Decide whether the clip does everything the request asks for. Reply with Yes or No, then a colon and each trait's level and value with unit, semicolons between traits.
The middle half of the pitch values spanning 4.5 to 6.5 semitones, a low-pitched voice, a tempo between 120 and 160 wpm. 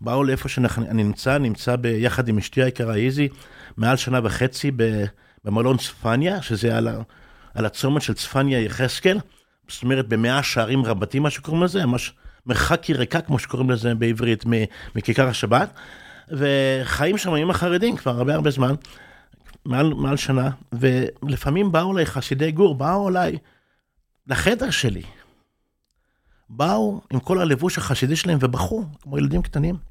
No: average, 4.1 semitones; low, 130 Hz; average, 135 wpm